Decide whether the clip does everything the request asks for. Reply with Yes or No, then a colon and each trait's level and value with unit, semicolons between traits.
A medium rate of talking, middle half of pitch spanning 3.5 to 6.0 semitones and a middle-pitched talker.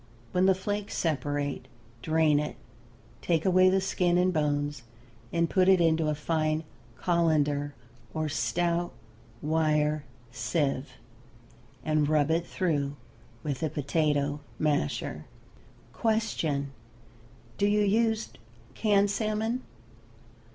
No: slow, 110 wpm; average, 4.1 semitones; medium, 160 Hz